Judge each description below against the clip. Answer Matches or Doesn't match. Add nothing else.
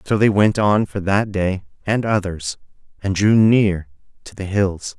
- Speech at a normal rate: Matches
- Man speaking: Matches